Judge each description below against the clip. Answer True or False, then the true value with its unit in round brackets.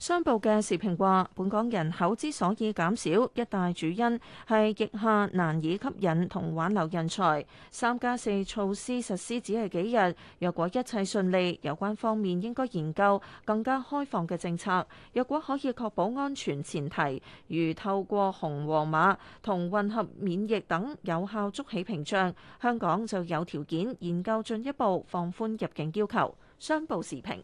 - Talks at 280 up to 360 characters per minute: False (245 characters per minute)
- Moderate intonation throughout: True (4.3 semitones)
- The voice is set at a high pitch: True (200 Hz)